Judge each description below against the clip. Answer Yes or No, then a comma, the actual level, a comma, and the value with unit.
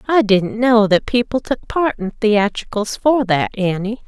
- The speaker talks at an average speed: Yes, average, 175 wpm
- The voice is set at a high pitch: Yes, high, 220 Hz